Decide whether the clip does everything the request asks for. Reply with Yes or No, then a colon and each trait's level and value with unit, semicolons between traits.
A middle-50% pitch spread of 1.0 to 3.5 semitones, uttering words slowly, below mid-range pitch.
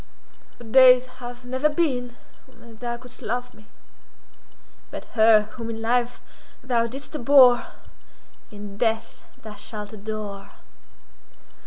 No: narrow, 2.4 semitones; slow, 115 wpm; high, 235 Hz